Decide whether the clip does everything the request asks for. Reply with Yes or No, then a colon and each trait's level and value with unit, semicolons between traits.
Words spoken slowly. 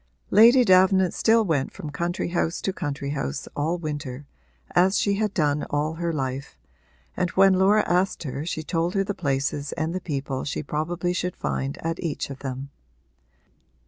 No: average, 175 wpm